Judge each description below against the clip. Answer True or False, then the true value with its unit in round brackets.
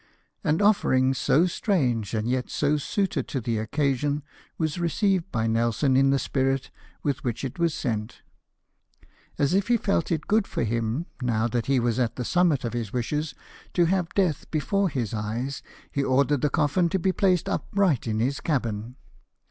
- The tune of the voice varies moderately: False (6.1 semitones)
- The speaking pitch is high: False (140 Hz)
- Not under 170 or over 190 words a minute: True (180 wpm)